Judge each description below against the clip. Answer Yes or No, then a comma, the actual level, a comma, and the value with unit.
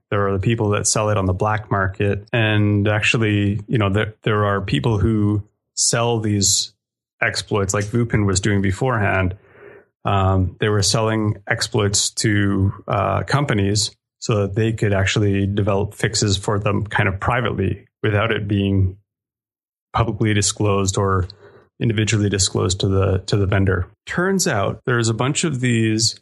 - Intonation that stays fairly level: Yes, narrow, 2.3 semitones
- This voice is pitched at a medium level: No, low, 105 Hz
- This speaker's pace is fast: No, average, 160 wpm